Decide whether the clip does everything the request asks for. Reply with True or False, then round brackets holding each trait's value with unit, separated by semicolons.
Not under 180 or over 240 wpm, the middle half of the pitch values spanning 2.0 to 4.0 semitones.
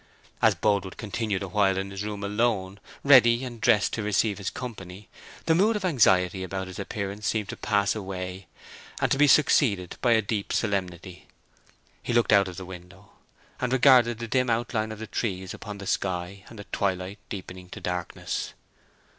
False (170 wpm; 3.5 semitones)